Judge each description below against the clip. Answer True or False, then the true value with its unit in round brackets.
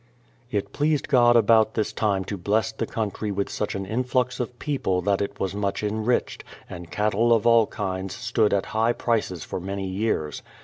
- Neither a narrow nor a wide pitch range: True (3.0 semitones)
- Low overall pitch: True (105 Hz)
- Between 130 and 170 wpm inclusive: False (185 wpm)